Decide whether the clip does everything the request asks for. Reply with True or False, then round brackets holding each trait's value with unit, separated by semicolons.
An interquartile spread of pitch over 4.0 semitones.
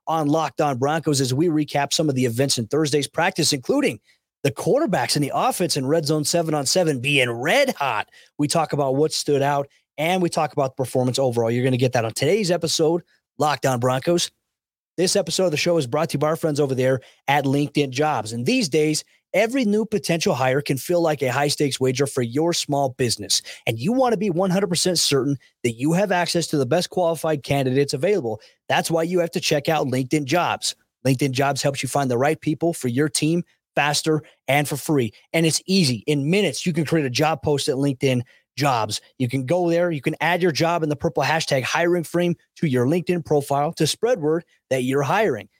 False (3.4 semitones)